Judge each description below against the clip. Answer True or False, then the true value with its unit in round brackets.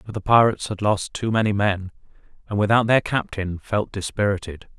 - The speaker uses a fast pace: False (175 wpm)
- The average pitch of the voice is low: True (105 Hz)